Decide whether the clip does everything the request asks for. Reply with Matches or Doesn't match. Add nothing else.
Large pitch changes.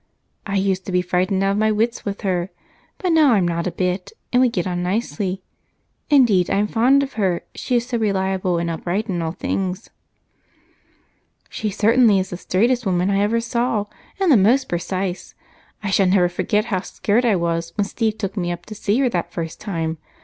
Doesn't match